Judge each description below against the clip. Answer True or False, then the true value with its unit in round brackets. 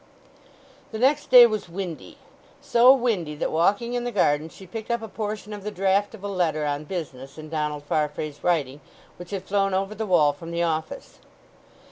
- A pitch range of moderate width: False (5.8 semitones)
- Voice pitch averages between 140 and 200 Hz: True (190 Hz)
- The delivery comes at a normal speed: True (185 wpm)